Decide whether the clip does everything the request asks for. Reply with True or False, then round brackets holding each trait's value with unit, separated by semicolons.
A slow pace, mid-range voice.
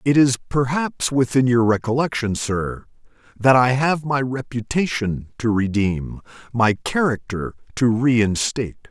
False (120 wpm; 120 Hz)